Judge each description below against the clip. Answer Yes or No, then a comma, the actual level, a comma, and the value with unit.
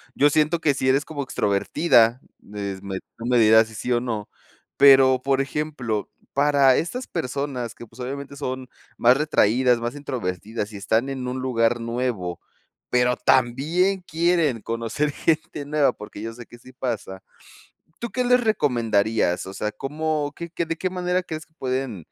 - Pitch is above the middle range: No, low, 130 Hz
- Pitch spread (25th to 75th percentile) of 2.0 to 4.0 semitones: No, average, 4.6 semitones